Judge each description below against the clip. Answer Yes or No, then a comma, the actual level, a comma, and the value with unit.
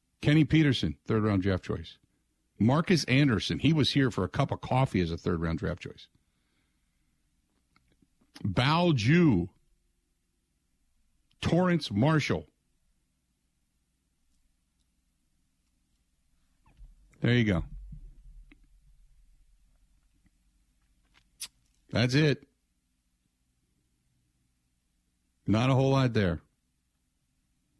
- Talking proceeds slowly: Yes, slow, 80 wpm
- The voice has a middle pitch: No, very low, 80 Hz